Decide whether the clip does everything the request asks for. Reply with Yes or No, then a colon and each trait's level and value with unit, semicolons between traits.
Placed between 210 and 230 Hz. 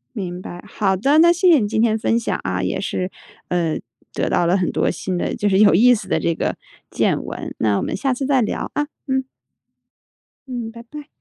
Yes: high, 215 Hz